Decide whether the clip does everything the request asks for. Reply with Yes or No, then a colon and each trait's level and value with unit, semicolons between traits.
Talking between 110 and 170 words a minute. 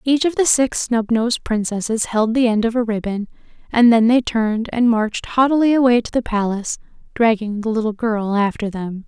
No: average, 190 wpm